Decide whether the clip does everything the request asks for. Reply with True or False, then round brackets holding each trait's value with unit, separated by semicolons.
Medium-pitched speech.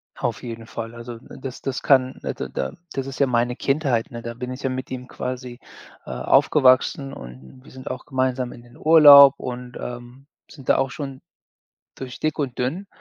False (130 Hz)